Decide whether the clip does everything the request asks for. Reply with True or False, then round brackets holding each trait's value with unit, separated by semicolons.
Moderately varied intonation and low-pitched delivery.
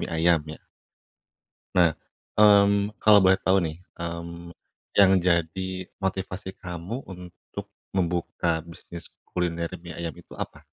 False (2.0 semitones; 85 Hz)